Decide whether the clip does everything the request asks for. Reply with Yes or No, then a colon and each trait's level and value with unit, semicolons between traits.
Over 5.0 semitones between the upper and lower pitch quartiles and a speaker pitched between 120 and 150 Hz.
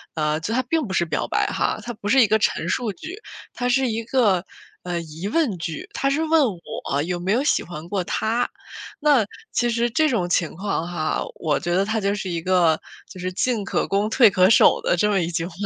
No: wide, 5.5 semitones; high, 200 Hz